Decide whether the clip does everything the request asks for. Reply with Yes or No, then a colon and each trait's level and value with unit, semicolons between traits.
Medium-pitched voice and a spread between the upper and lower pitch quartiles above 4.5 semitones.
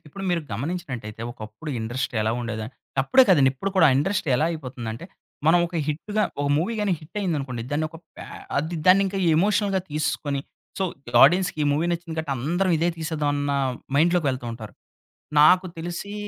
Yes: medium, 155 Hz; average, 5.1 semitones